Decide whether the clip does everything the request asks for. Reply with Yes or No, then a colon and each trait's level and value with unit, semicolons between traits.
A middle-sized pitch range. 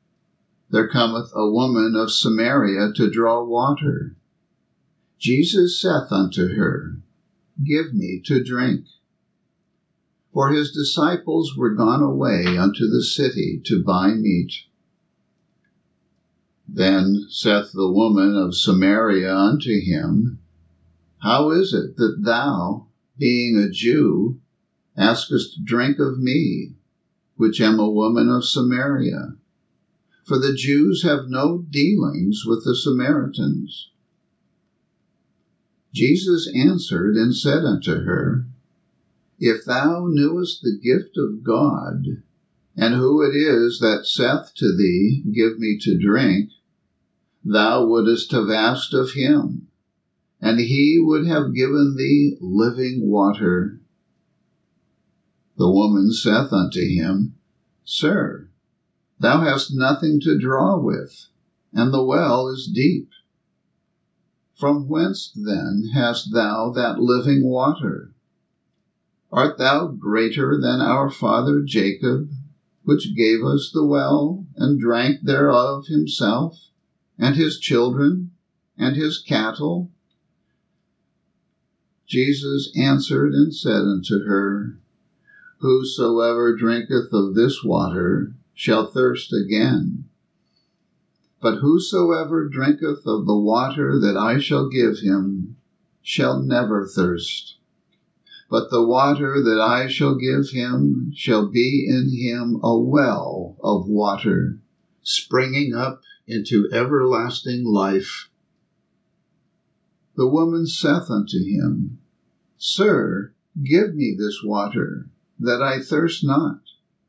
Yes: average, 4.9 semitones